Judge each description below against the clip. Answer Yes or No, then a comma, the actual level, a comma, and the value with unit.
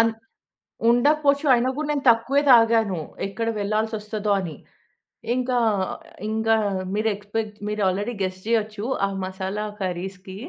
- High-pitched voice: Yes, high, 215 Hz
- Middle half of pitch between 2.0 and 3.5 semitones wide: Yes, average, 2.9 semitones